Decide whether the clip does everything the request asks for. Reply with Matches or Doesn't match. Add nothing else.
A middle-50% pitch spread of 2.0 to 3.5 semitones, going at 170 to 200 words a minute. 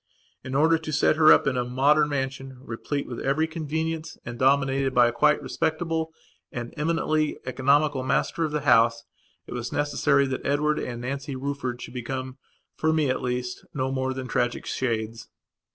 Matches